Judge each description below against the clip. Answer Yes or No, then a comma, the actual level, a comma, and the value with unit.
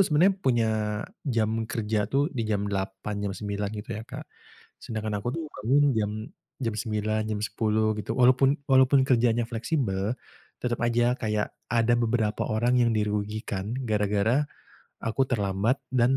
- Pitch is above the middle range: No, low, 110 Hz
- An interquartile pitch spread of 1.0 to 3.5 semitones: Yes, narrow, 2.5 semitones